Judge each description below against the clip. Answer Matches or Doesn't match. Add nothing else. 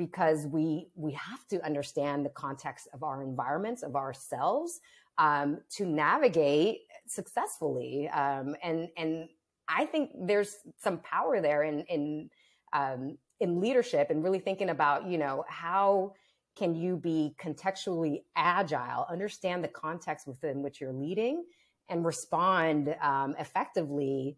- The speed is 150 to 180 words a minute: Doesn't match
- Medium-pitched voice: Matches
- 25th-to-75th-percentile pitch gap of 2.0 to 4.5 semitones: Doesn't match